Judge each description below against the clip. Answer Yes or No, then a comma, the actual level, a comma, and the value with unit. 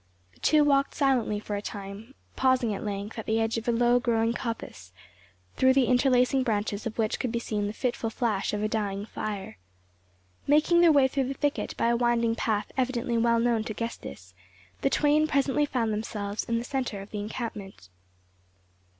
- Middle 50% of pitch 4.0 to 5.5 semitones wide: No, average, 3.6 semitones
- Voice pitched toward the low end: No, high, 230 Hz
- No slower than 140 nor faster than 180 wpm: No, average, 190 wpm